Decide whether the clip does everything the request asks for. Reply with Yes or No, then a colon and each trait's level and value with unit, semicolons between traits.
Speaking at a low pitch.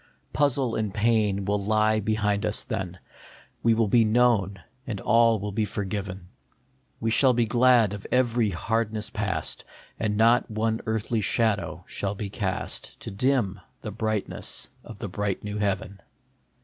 Yes: low, 110 Hz